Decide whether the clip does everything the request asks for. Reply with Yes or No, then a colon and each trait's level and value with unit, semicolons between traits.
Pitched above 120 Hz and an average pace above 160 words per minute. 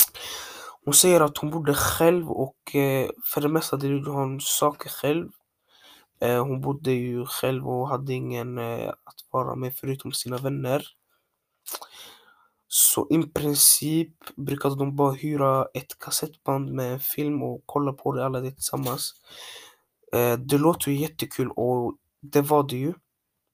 No: medium, 140 Hz; average, 150 wpm